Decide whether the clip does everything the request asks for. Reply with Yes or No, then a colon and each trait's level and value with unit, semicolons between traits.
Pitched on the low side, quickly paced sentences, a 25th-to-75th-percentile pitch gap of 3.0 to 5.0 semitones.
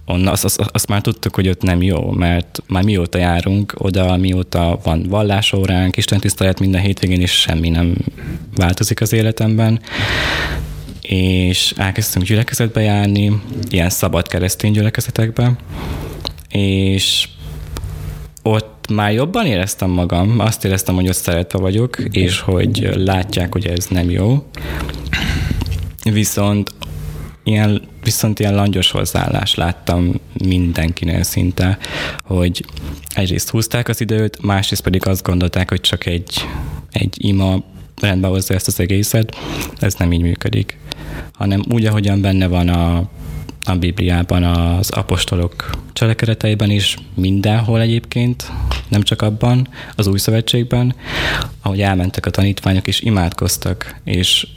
No: very low, 95 Hz; average, 125 wpm; average, 3.5 semitones